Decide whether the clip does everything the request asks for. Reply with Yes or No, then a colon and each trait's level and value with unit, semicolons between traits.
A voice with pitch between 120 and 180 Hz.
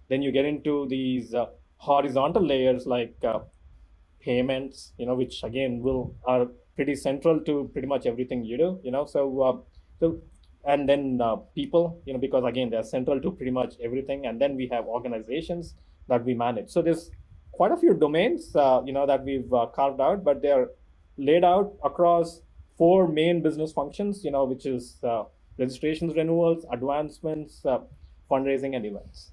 Yes: low, 135 Hz